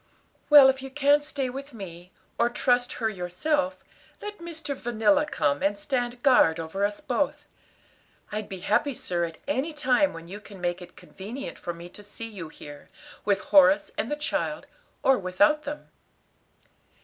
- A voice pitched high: Yes, high, 230 Hz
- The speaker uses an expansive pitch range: Yes, wide, 7.4 semitones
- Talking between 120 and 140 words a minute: No, average, 170 wpm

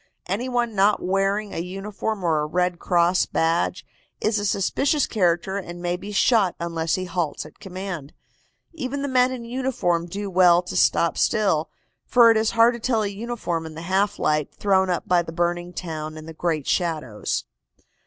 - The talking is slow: No, average, 185 wpm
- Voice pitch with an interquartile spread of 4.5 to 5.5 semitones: No, average, 4.0 semitones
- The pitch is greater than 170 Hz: Yes, medium, 185 Hz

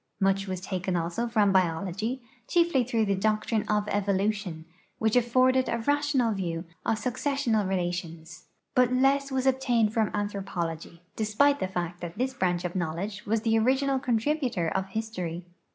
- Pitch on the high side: Yes, high, 210 Hz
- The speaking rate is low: No, average, 150 wpm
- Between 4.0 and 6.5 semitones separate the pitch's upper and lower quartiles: Yes, wide, 5.4 semitones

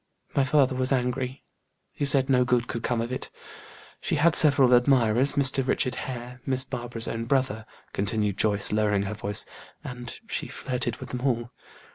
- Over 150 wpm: Yes, average, 170 wpm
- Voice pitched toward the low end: Yes, low, 125 Hz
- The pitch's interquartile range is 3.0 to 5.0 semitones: No, narrow, 2.4 semitones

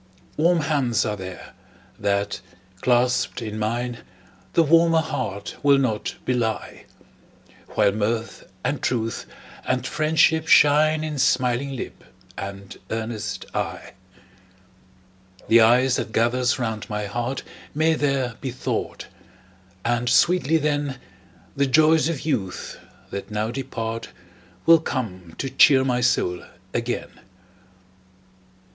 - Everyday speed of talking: No, slow, 115 wpm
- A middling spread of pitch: Yes, average, 4.7 semitones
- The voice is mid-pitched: No, low, 125 Hz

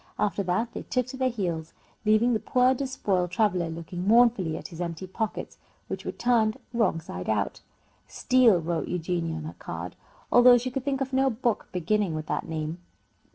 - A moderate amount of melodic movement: No, wide, 6.4 semitones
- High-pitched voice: Yes, high, 205 Hz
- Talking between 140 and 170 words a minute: No, average, 185 wpm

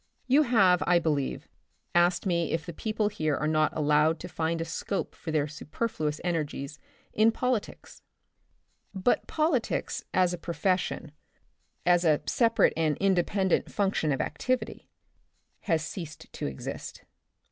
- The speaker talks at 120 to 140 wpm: Yes, slow, 135 wpm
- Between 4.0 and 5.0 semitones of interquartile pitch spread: Yes, average, 4.3 semitones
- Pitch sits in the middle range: Yes, medium, 175 Hz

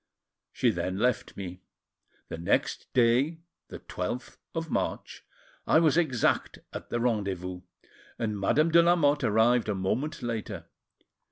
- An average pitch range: No, wide, 6.9 semitones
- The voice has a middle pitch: No, low, 120 Hz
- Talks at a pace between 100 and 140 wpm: Yes, slow, 135 wpm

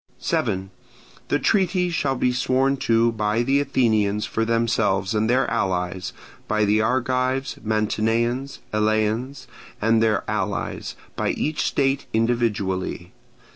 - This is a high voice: No, low, 115 Hz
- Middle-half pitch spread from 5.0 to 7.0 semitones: No, average, 3.4 semitones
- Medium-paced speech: No, slow, 120 wpm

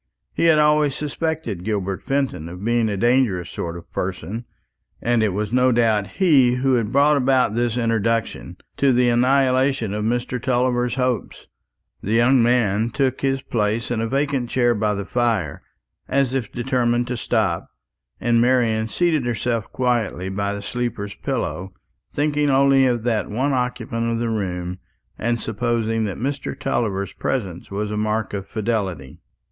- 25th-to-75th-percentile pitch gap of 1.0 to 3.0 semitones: No, average, 3.5 semitones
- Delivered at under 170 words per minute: Yes, average, 160 wpm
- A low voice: Yes, low, 120 Hz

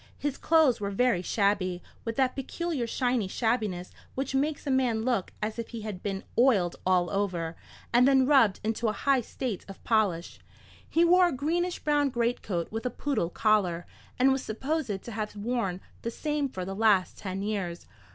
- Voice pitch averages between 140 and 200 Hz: No, high, 225 Hz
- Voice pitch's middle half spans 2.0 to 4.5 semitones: No, average, 5.3 semitones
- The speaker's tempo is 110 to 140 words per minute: No, average, 180 wpm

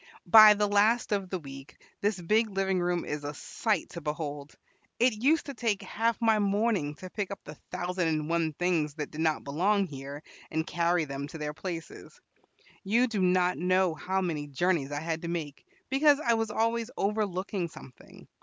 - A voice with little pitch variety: No, average, 5.1 semitones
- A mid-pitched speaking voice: Yes, medium, 180 Hz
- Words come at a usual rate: Yes, average, 190 wpm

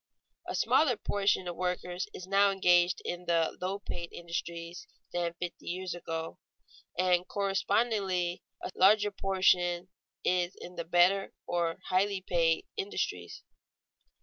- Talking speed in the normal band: No, slow, 130 wpm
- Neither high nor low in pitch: Yes, medium, 180 Hz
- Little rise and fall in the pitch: Yes, narrow, 2.0 semitones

